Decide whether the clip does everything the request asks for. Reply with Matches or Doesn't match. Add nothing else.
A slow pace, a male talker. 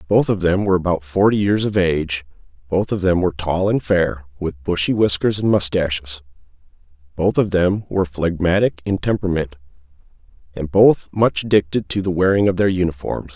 Doesn't match